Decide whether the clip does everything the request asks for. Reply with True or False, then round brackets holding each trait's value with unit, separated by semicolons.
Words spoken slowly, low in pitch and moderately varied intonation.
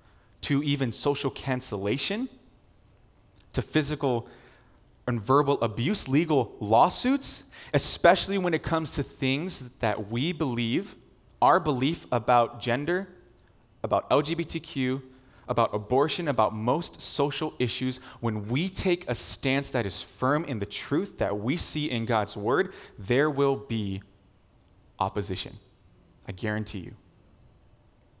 True (120 wpm; 125 Hz; 4.7 semitones)